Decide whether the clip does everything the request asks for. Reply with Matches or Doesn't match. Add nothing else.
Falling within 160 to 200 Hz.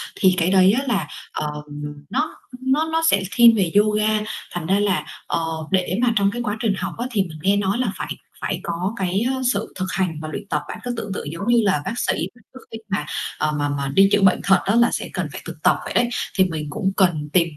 Matches